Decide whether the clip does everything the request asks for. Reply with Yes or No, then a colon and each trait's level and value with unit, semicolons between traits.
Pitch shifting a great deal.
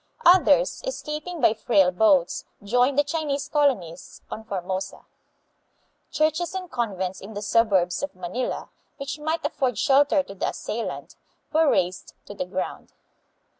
Yes: wide, 7.5 semitones